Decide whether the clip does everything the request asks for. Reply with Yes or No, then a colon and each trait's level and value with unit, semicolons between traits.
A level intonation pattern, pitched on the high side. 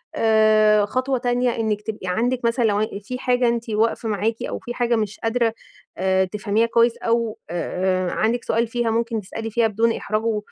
Yes: narrow, 1.9 semitones; high, 225 Hz